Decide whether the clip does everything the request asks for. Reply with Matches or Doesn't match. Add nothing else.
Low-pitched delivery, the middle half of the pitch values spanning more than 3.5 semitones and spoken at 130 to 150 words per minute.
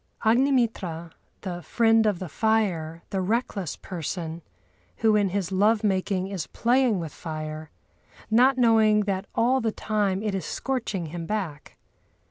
Doesn't match